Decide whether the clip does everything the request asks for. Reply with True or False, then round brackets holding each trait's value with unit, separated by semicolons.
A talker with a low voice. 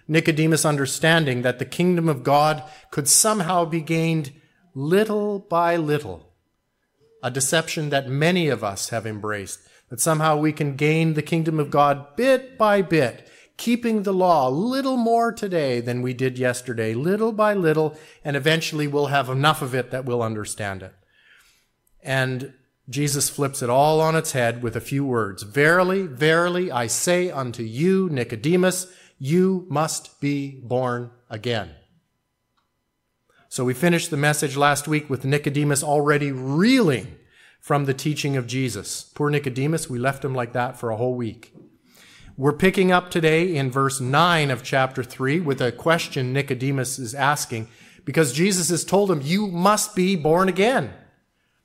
False (145 Hz)